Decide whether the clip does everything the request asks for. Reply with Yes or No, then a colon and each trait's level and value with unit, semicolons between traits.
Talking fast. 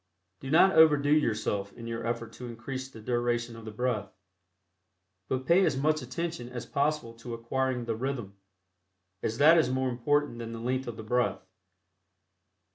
No: average, 170 wpm